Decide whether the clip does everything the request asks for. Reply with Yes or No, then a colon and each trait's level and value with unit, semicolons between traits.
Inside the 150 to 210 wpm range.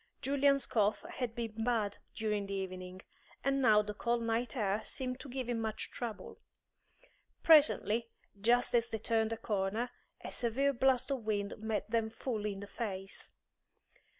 Yes: average, 160 wpm